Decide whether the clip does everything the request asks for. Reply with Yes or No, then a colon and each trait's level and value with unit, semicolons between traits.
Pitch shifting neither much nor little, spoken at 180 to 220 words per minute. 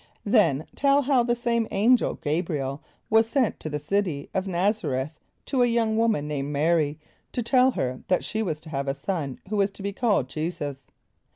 No: wide, 7.5 semitones; average, 200 wpm